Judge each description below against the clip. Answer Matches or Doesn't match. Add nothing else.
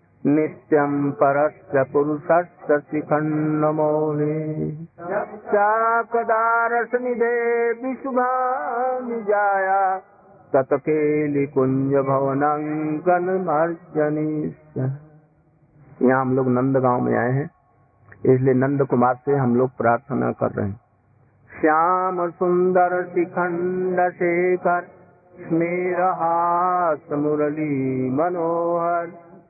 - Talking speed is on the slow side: Matches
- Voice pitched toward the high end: Doesn't match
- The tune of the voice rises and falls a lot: Doesn't match